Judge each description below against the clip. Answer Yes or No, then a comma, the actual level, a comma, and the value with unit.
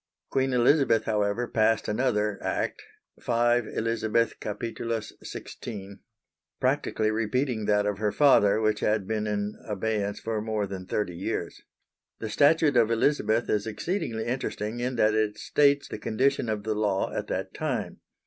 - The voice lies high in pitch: No, low, 110 Hz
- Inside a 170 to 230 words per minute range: No, average, 150 wpm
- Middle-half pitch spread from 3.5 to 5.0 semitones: No, narrow, 2.4 semitones